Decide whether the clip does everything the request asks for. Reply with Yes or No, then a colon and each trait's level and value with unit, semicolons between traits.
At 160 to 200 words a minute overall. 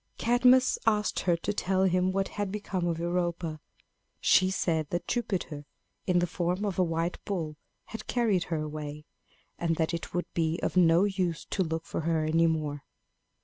Yes: average, 180 wpm